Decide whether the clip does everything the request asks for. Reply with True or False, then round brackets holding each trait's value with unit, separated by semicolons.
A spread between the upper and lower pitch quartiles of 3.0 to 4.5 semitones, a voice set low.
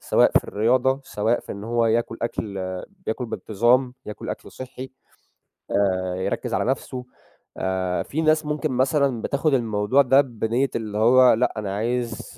True (3.7 semitones; 120 Hz)